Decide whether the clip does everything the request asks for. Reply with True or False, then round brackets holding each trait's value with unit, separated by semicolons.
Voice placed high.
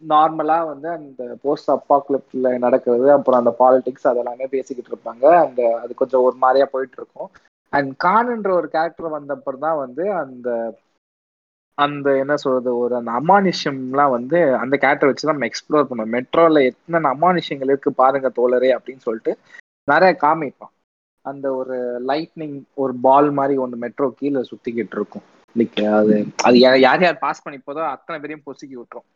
False (135 Hz)